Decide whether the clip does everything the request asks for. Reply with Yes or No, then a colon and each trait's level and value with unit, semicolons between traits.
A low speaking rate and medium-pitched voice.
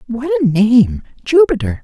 No: slow, 100 wpm; high, 220 Hz